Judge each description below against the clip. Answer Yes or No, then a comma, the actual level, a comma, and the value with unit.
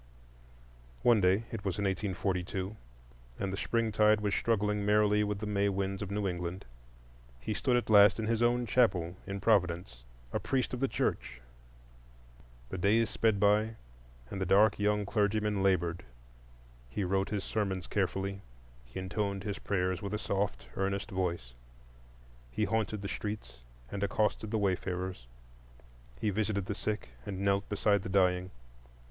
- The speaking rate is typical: Yes, average, 150 wpm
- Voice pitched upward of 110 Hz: No, low, 100 Hz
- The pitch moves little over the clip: Yes, narrow, 2.3 semitones